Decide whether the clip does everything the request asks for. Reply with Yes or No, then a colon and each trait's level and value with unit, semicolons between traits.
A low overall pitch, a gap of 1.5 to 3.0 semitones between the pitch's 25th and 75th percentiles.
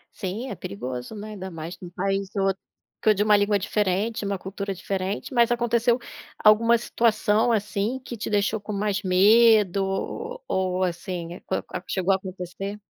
No: high, 200 Hz; narrow, 2.6 semitones